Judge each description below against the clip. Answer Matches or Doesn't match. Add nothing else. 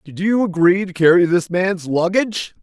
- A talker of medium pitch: Matches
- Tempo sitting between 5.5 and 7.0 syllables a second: Doesn't match